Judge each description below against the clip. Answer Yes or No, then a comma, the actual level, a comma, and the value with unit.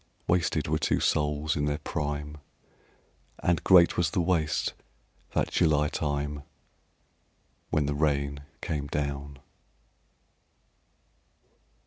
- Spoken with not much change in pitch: Yes, narrow, 1.4 semitones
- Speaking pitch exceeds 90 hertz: No, very low, 75 Hz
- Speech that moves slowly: Yes, slow, 100 wpm